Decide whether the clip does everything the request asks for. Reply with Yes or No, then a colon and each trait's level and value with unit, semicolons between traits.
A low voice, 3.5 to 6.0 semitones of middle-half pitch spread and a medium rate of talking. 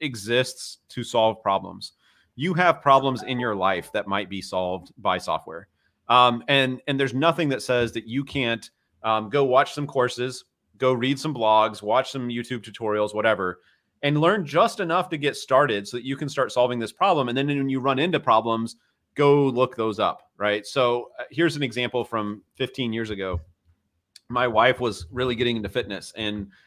Yes: low, 120 Hz; average, 4.2 semitones; average, 185 wpm